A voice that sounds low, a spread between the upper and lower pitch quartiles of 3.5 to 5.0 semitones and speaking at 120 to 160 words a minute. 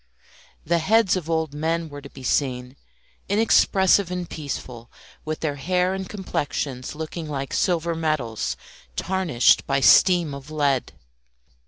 No: medium, 155 Hz; average, 4.5 semitones; slow, 135 wpm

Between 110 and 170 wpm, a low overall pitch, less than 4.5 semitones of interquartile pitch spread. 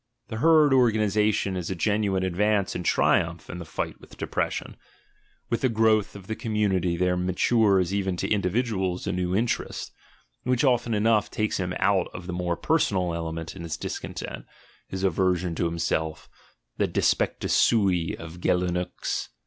Yes: average, 160 wpm; very low, 95 Hz; average, 3.4 semitones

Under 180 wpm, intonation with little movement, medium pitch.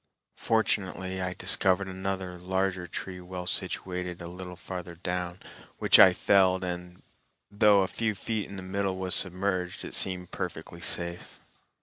No: average, 145 wpm; narrow, 1.1 semitones; very low, 95 Hz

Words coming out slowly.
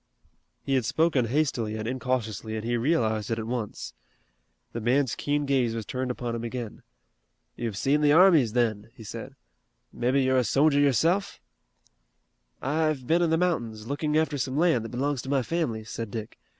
No: average, 175 wpm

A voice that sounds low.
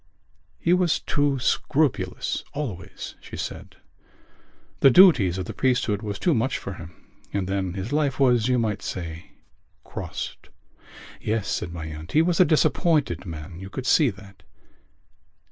Yes: low, 110 Hz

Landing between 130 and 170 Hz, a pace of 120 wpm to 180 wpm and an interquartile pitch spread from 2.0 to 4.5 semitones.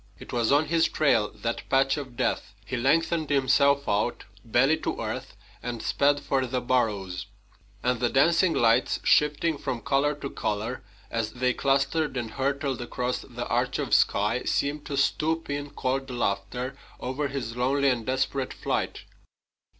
Yes: low, 135 Hz; average, 160 wpm; average, 2.9 semitones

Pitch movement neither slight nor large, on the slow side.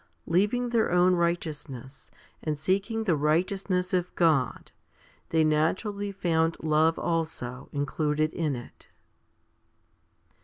Yes: average, 3.3 semitones; slow, 105 wpm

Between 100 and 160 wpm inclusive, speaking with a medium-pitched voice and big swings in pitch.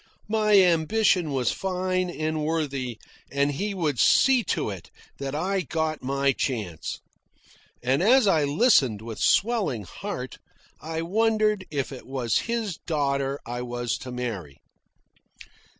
Yes: slow, 135 wpm; medium, 150 Hz; wide, 6.8 semitones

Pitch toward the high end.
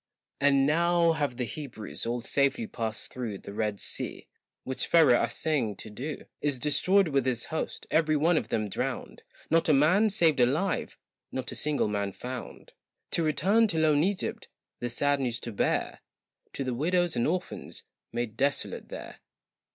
No: medium, 145 Hz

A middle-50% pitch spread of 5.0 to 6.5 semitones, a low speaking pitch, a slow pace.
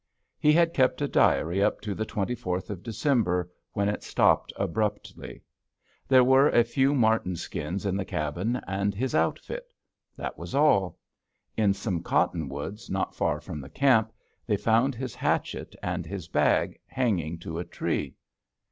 No: wide, 5.6 semitones; low, 105 Hz; average, 155 wpm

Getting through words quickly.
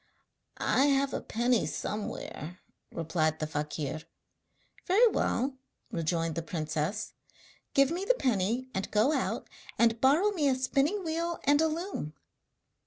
No: slow, 135 wpm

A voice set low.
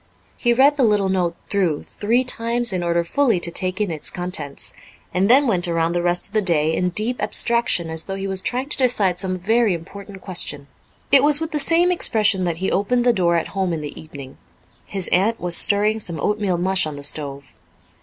No: high, 190 Hz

